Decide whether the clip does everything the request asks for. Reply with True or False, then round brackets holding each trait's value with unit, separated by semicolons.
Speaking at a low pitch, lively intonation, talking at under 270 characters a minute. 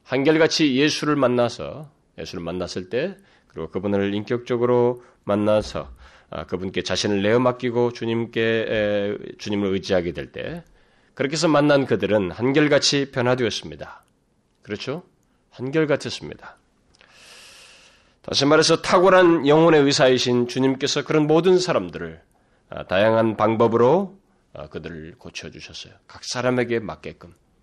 False (125 Hz; 5.9 semitones; 305 characters per minute)